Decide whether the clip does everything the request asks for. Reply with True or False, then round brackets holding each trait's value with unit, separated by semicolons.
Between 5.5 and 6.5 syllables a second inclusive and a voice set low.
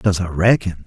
False (4.8 syllables/s; 95 Hz)